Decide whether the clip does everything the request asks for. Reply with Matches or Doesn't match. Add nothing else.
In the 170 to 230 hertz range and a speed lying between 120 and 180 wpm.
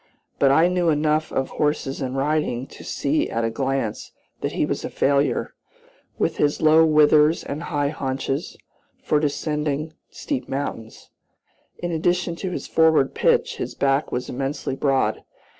Doesn't match